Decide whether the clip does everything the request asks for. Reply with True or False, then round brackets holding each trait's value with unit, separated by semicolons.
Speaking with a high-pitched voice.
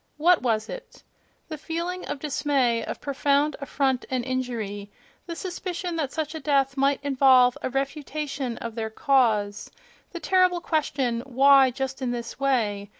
True (275 Hz)